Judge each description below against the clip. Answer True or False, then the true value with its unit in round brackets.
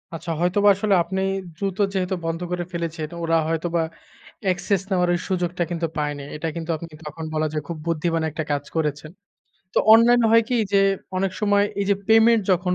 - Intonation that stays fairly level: False (3.0 semitones)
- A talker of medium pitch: True (175 Hz)